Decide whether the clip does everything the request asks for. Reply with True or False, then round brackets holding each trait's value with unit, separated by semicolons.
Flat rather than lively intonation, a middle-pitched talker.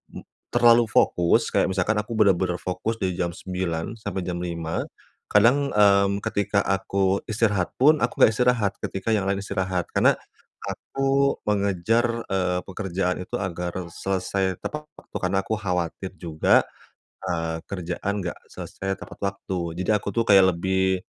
False (2.3 semitones; 95 Hz)